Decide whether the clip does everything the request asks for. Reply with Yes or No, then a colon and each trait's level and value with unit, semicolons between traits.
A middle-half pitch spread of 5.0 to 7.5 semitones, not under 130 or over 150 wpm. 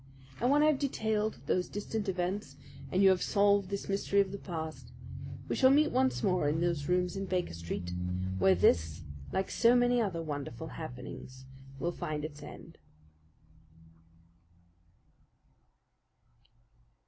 Yes: wide, 5.5 semitones; average, 140 wpm